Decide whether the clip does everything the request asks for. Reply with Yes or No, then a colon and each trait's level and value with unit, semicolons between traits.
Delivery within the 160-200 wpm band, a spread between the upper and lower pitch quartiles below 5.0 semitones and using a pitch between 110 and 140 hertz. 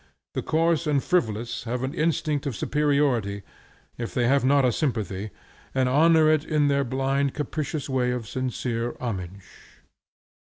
No: average, 150 wpm; average, 3.8 semitones; low, 135 Hz